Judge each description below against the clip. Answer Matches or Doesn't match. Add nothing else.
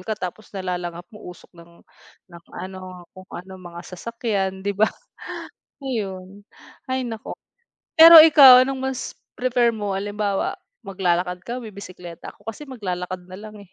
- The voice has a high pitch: Matches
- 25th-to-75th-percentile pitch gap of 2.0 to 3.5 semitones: Doesn't match